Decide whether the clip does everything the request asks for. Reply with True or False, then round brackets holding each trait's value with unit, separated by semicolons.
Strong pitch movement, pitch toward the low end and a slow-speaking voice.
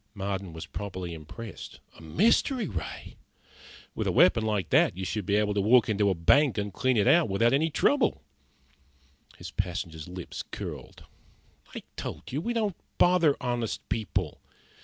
False (6.9 semitones; 105 Hz; 160 wpm)